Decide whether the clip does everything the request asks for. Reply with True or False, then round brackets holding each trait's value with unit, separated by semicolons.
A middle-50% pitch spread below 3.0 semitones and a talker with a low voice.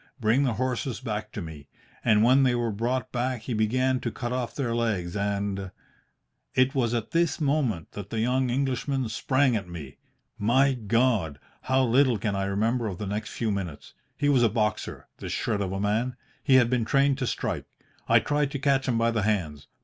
False (4.1 semitones; 115 Hz)